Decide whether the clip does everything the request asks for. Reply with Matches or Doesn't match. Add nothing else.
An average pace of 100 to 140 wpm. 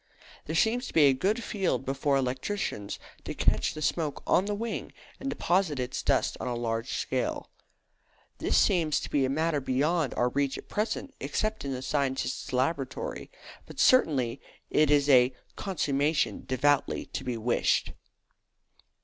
Doesn't match